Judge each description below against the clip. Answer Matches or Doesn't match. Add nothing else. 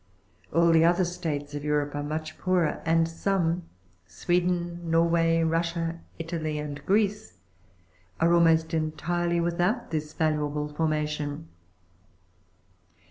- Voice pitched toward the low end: Doesn't match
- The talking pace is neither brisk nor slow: Doesn't match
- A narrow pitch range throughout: Matches